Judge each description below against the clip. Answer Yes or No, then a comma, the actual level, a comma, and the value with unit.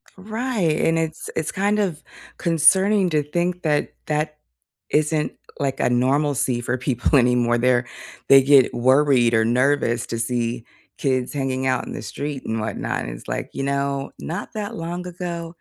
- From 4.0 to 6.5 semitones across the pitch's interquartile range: Yes, average, 5.1 semitones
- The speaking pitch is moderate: Yes, medium, 145 Hz